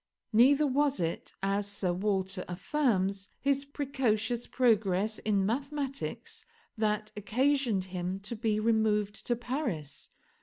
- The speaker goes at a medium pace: No, slow, 115 wpm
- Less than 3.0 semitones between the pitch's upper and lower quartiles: No, average, 5.1 semitones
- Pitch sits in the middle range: No, high, 215 Hz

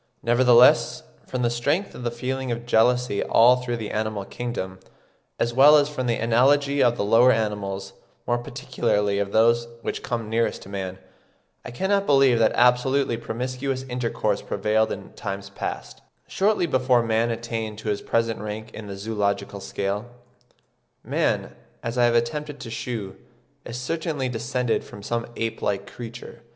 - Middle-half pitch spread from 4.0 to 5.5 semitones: No, average, 2.7 semitones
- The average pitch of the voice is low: Yes, low, 120 Hz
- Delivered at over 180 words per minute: No, average, 160 wpm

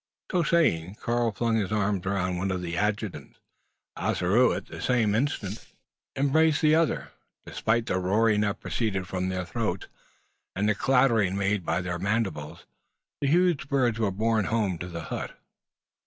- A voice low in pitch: Yes, low, 105 Hz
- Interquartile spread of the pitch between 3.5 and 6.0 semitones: Yes, average, 4.3 semitones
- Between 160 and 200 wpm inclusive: Yes, average, 165 wpm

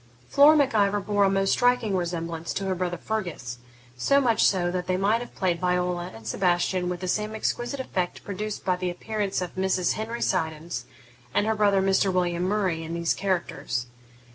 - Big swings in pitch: No, average, 3.1 semitones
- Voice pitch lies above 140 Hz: Yes, medium, 185 Hz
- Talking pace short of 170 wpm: No, average, 190 wpm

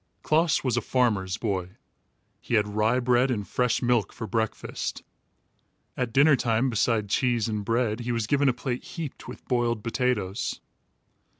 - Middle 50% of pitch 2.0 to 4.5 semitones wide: Yes, average, 2.8 semitones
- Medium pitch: No, low, 120 Hz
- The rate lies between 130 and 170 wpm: Yes, average, 160 wpm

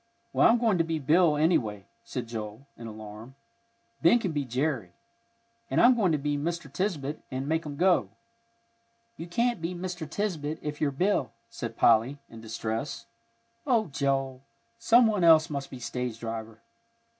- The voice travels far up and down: Yes, wide, 6.2 semitones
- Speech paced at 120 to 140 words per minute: No, average, 165 wpm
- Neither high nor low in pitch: Yes, medium, 145 Hz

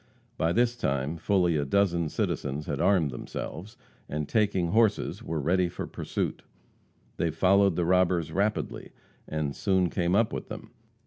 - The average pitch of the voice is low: Yes, very low, 90 Hz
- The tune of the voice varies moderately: Yes, average, 4.2 semitones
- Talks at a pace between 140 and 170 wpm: Yes, average, 150 wpm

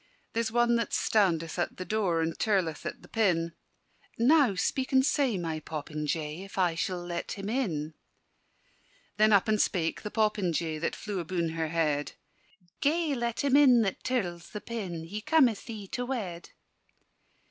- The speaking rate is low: No, average, 165 wpm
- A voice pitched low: No, high, 195 Hz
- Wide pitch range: Yes, wide, 5.8 semitones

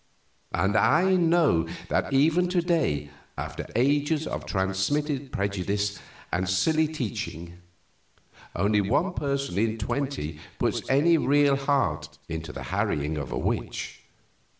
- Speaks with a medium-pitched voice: No, low, 130 Hz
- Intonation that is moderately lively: No, wide, 7.8 semitones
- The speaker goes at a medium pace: No, slow, 125 wpm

